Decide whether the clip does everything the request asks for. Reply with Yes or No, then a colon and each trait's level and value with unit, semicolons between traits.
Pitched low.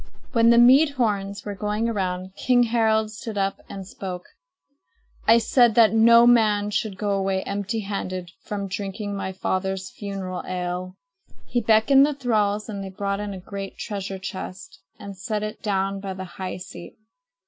No: high, 200 Hz